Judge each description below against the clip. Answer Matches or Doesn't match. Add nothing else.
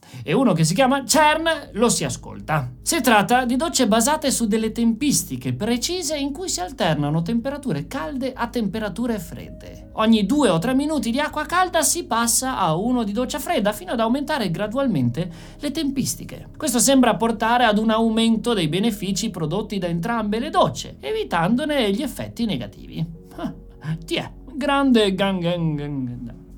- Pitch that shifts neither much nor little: Doesn't match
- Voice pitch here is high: Matches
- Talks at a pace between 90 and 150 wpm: Doesn't match